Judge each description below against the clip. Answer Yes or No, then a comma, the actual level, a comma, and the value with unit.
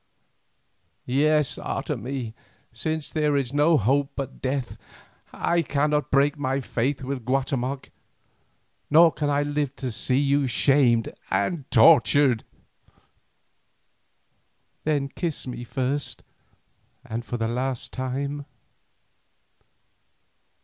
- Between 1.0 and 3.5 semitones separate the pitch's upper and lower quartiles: Yes, narrow, 2.5 semitones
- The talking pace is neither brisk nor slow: No, slow, 100 wpm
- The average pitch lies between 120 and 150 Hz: Yes, low, 135 Hz